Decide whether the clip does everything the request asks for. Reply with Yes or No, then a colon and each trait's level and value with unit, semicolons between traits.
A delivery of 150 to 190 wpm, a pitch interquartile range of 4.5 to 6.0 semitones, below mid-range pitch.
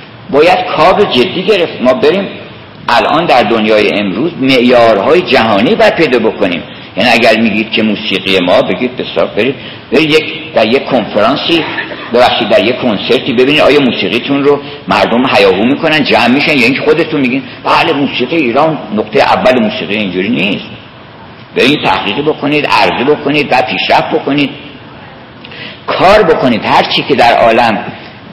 Yes: fast, 155 wpm; average, 5.2 semitones; low, 130 Hz